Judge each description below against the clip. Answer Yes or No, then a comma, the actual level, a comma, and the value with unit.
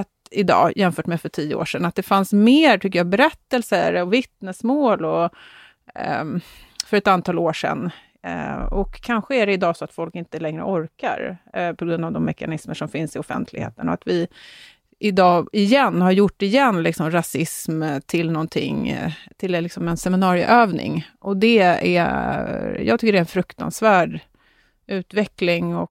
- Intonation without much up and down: No, average, 3.5 semitones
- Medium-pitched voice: Yes, medium, 180 Hz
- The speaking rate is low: No, average, 165 wpm